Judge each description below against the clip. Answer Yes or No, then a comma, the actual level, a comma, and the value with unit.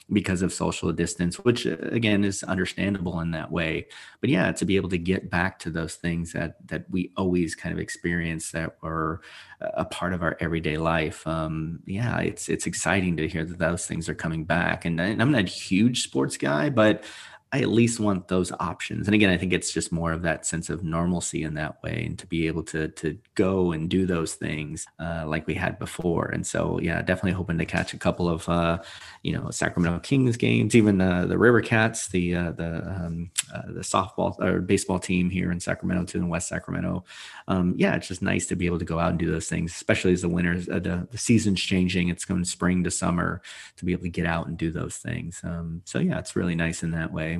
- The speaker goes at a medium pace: No, fast, 235 wpm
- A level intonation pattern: Yes, narrow, 2.1 semitones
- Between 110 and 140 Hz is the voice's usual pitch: No, very low, 85 Hz